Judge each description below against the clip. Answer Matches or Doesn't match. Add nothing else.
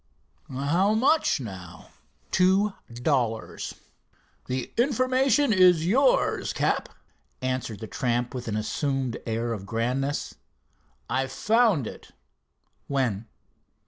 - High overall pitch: Doesn't match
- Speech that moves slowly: Matches